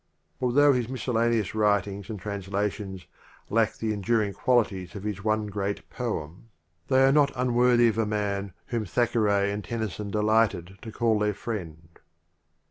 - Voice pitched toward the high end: No, low, 105 Hz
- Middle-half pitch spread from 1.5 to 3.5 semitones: Yes, average, 2.8 semitones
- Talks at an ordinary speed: Yes, average, 145 wpm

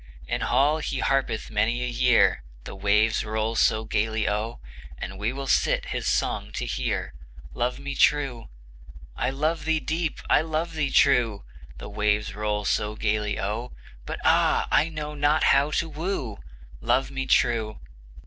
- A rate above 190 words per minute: No, average, 160 wpm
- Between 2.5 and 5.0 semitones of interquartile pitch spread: No, wide, 5.4 semitones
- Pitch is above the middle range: No, low, 120 Hz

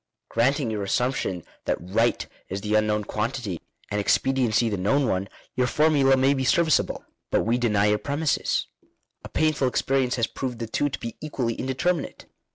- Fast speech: No, average, 165 wpm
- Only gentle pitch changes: No, average, 4.3 semitones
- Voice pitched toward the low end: Yes, low, 125 Hz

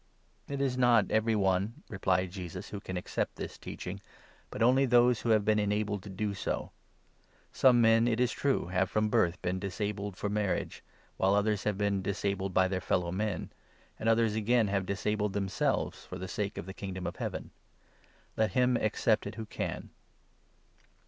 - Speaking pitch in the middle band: No, low, 105 Hz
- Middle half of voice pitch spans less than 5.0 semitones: Yes, average, 2.8 semitones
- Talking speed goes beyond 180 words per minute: Yes, average, 190 wpm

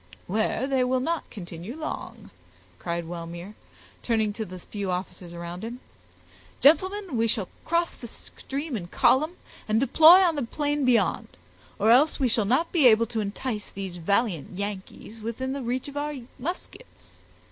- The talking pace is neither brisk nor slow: Yes, average, 160 wpm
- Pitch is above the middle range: Yes, high, 230 Hz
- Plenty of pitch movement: Yes, wide, 6.1 semitones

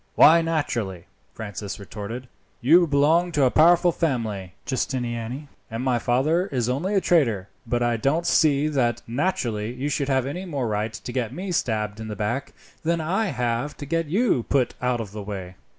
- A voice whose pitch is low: Yes, low, 125 Hz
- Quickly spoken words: No, average, 180 wpm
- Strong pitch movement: Yes, wide, 5.9 semitones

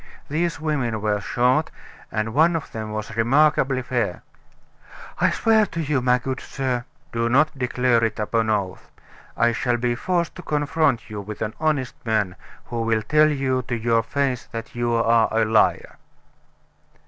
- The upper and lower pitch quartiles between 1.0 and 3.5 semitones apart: No, average, 4.1 semitones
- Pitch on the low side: Yes, low, 120 Hz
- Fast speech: No, average, 170 wpm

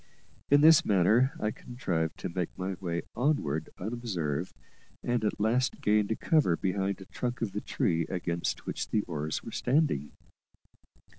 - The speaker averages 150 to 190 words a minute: Yes, average, 155 wpm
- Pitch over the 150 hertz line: No, low, 100 Hz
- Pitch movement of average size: No, wide, 6.0 semitones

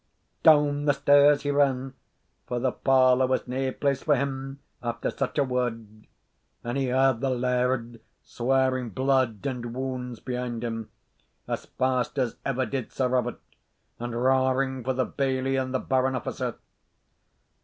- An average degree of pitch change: No, narrow, 1.5 semitones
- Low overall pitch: Yes, low, 130 Hz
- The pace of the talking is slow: No, average, 150 wpm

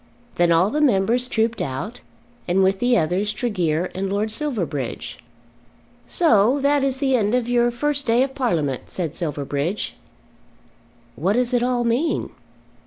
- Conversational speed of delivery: Yes, average, 150 wpm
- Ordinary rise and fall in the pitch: No, wide, 5.9 semitones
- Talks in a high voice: Yes, high, 220 Hz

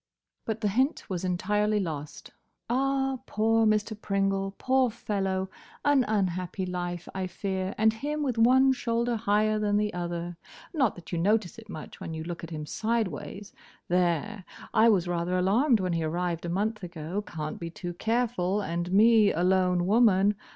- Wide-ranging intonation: No, average, 4.0 semitones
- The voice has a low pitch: No, high, 195 Hz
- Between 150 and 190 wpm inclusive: Yes, average, 170 wpm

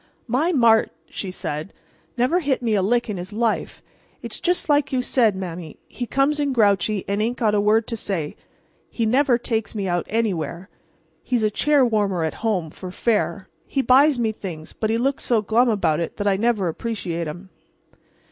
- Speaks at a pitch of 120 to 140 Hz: No, high, 220 Hz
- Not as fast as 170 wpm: No, average, 195 wpm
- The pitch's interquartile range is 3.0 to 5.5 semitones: Yes, average, 4.3 semitones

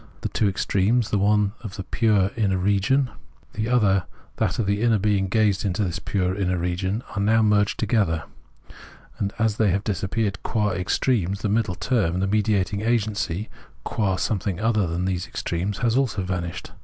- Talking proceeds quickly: No, average, 180 wpm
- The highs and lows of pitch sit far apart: No, average, 2.7 semitones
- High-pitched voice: No, low, 100 Hz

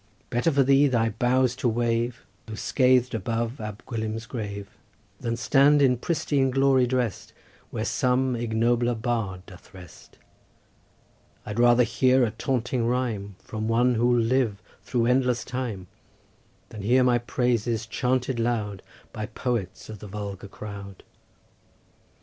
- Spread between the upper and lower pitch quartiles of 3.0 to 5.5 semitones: No, narrow, 2.6 semitones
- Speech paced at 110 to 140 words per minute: Yes, slow, 135 wpm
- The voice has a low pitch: Yes, low, 120 Hz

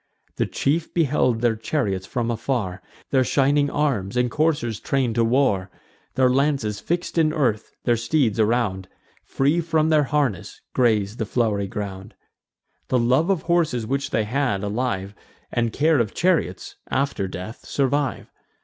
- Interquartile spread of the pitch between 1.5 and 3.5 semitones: No, average, 5.1 semitones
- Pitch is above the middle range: No, low, 125 Hz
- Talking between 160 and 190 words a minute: No, average, 150 wpm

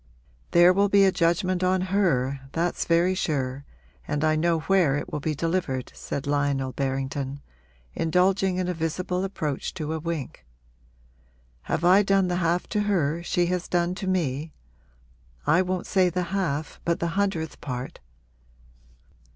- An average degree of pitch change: Yes, average, 4.0 semitones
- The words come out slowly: No, average, 155 wpm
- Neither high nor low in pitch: Yes, medium, 170 Hz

